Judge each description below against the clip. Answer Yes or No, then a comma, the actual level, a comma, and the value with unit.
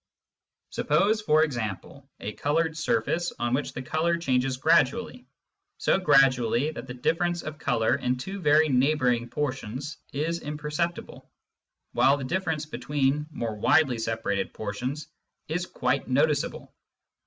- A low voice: No, medium, 145 Hz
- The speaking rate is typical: No, slow, 130 wpm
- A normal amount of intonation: Yes, average, 4.1 semitones